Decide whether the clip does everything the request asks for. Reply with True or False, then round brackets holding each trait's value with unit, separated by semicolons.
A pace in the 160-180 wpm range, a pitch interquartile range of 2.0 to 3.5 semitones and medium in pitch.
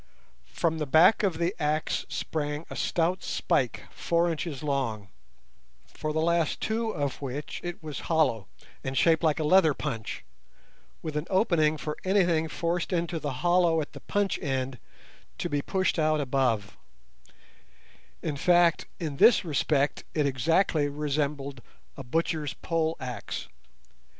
False (140 wpm; 3.2 semitones; 155 Hz)